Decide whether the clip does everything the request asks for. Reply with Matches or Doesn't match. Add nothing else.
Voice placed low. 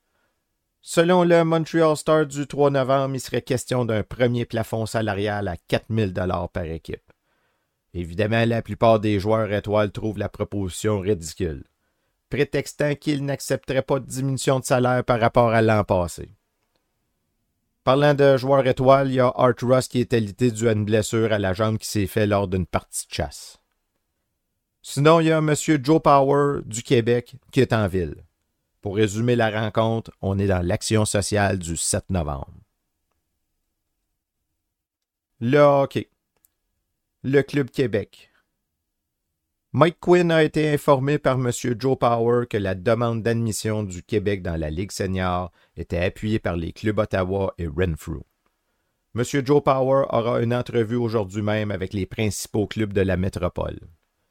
Matches